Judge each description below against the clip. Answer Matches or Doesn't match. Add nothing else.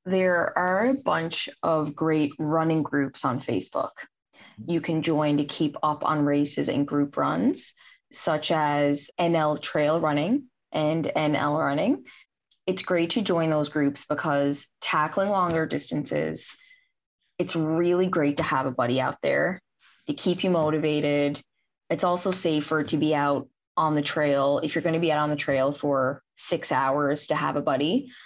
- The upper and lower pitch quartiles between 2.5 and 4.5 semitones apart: Matches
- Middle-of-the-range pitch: Matches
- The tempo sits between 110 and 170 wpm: Matches